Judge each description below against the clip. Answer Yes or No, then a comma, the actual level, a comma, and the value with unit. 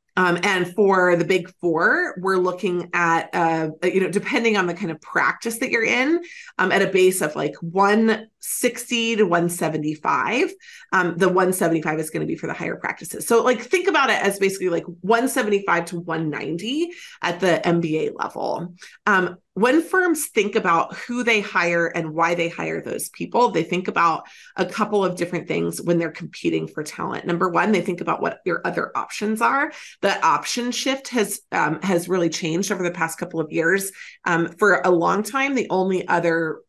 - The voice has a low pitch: No, medium, 185 Hz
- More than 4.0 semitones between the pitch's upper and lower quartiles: Yes, average, 5.1 semitones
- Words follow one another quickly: No, average, 190 wpm